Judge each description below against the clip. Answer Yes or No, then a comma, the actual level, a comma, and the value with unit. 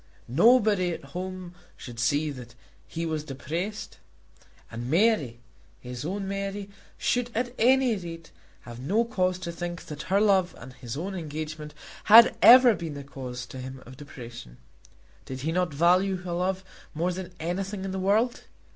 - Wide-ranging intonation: Yes, wide, 5.7 semitones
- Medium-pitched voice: Yes, medium, 175 Hz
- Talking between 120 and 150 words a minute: No, average, 165 wpm